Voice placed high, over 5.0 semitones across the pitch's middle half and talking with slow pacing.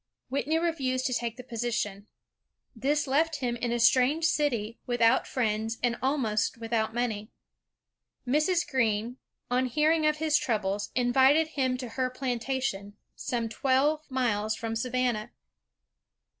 No: very high, 250 Hz; average, 3.3 semitones; slow, 130 wpm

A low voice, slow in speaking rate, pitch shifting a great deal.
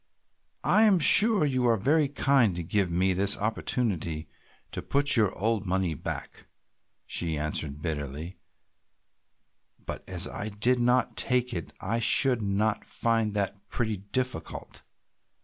Yes: low, 105 Hz; slow, 130 wpm; wide, 5.9 semitones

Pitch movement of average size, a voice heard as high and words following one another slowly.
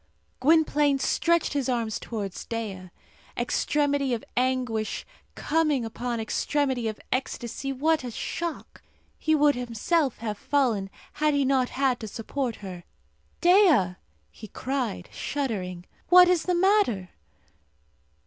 Yes: average, 4.8 semitones; very high, 255 Hz; slow, 120 wpm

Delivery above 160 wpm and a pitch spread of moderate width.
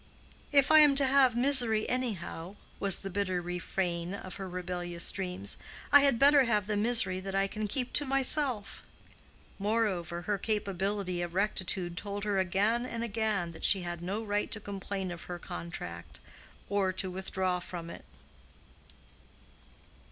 No: average, 155 wpm; average, 3.9 semitones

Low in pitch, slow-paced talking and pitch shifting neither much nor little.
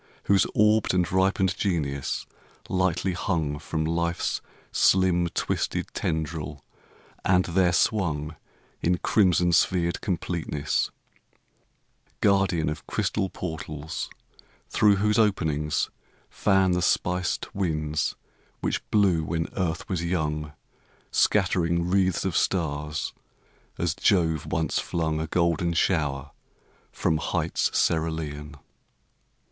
Yes: very low, 85 Hz; slow, 100 wpm; average, 3.1 semitones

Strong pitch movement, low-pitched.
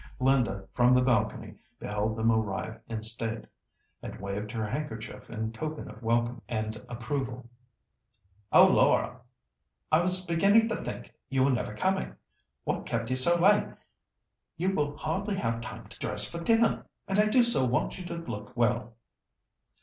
Yes: wide, 7.1 semitones; low, 125 Hz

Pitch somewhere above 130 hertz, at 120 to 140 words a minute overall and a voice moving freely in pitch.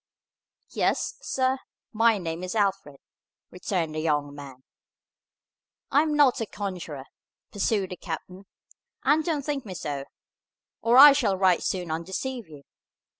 Yes: high, 190 Hz; slow, 135 wpm; wide, 7.6 semitones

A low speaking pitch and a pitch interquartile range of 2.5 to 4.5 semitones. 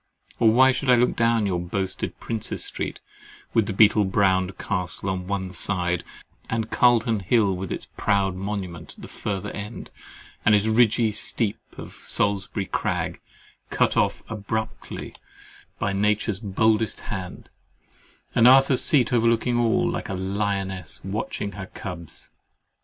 Yes: low, 100 Hz; average, 3.0 semitones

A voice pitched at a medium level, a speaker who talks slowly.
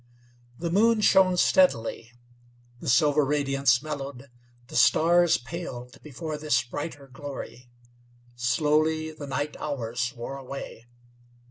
Yes: medium, 145 Hz; slow, 110 wpm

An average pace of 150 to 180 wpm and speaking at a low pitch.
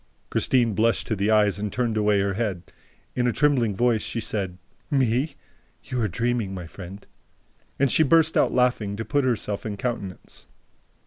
Yes: average, 175 wpm; low, 110 Hz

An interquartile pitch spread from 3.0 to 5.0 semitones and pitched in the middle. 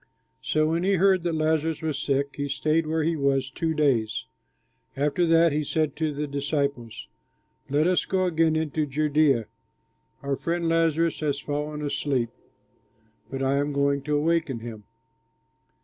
No: narrow, 2.5 semitones; medium, 150 Hz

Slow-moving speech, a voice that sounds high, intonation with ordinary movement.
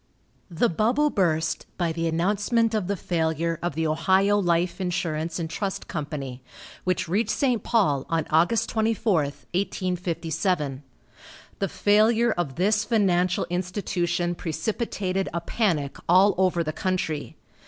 No: slow, 130 wpm; medium, 180 Hz; average, 3.9 semitones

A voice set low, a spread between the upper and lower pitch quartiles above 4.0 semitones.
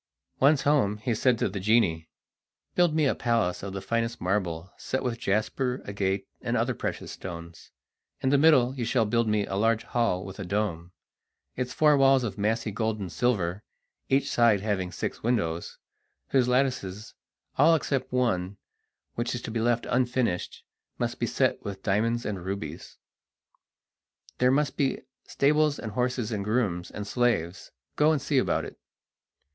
Yes: low, 115 Hz; average, 4.5 semitones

